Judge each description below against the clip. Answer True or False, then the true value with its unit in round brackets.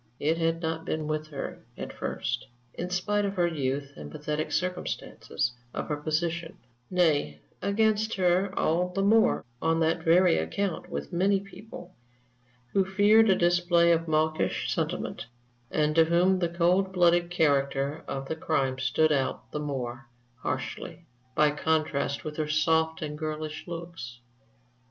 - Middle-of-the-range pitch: True (165 Hz)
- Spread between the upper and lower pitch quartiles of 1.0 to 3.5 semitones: True (3.1 semitones)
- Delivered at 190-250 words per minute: False (150 wpm)